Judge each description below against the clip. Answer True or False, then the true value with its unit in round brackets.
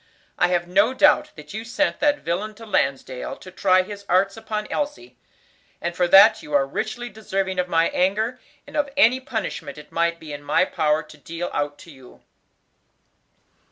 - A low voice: False (185 Hz)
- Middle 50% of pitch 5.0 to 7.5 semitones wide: True (5.5 semitones)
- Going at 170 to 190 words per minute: True (185 wpm)